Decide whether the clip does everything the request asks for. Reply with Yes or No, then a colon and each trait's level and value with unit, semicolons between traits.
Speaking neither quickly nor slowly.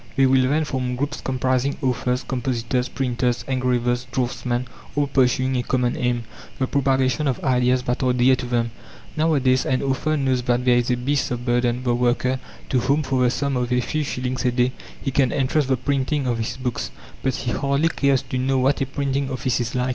No: fast, 210 wpm